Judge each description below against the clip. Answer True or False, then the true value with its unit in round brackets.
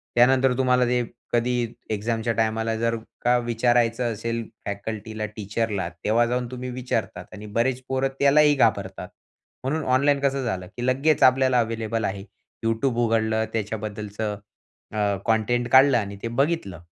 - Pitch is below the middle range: True (115 Hz)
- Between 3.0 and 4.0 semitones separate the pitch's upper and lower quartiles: False (2.5 semitones)